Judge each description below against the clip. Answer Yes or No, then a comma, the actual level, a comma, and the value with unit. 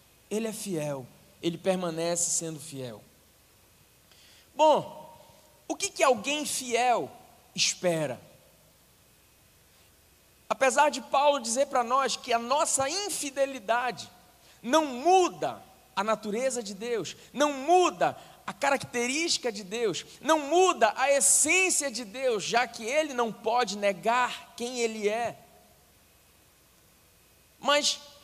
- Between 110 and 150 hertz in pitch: No, very high, 250 Hz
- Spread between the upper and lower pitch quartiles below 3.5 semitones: No, average, 4.7 semitones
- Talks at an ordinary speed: No, slow, 110 wpm